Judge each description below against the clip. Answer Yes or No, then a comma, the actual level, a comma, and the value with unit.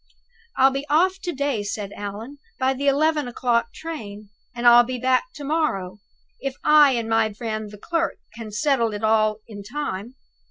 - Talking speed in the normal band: Yes, average, 175 wpm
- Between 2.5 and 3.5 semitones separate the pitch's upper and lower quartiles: No, average, 4.8 semitones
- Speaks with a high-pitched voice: Yes, high, 240 Hz